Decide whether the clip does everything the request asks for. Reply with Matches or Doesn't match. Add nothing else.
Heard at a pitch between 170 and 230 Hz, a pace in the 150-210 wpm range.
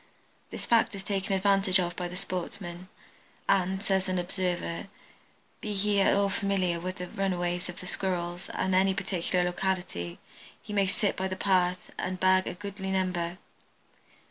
Matches